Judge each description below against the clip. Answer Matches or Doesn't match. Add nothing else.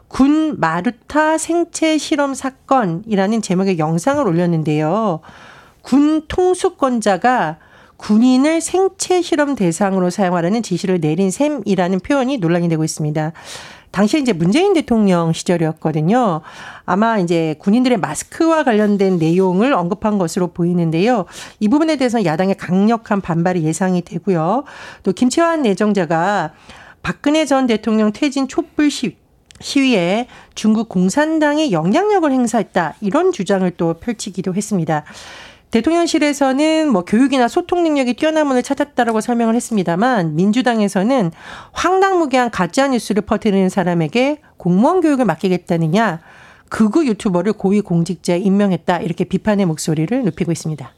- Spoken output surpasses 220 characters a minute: Matches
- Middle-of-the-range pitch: Doesn't match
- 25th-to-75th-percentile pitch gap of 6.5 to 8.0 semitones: Matches